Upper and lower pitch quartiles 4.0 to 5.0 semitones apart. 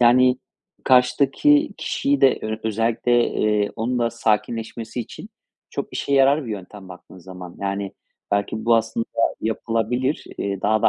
No: average, 3.3 semitones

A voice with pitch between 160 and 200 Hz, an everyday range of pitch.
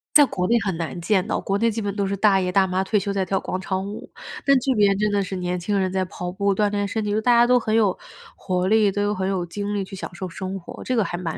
No: high, 195 Hz; narrow, 2.0 semitones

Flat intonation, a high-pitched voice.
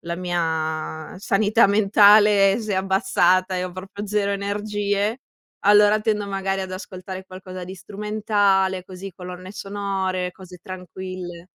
Yes: narrow, 1.8 semitones; high, 195 Hz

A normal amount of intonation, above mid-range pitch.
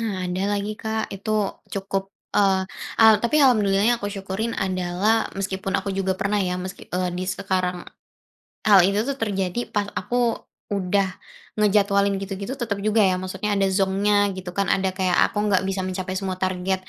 No: narrow, 1.8 semitones; high, 195 Hz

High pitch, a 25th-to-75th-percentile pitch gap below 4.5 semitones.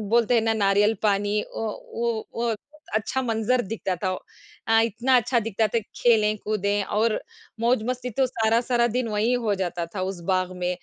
Yes: high, 220 Hz; narrow, 2.5 semitones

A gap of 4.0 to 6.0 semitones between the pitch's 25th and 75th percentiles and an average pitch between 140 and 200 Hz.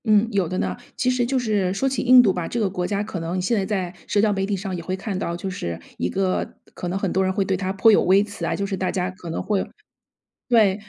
No: narrow, 2.4 semitones; high, 195 Hz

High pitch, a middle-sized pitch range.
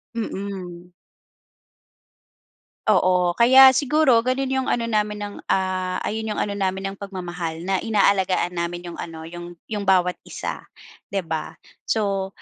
Yes: high, 195 Hz; average, 3.3 semitones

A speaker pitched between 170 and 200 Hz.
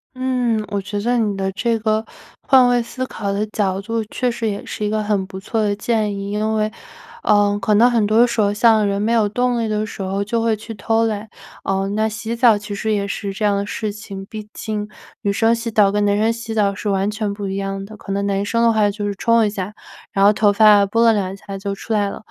No: high, 210 Hz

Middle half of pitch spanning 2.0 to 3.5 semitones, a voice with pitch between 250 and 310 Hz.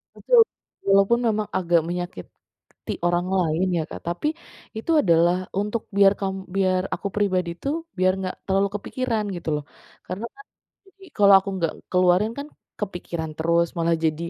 No: average, 3.2 semitones; medium, 185 Hz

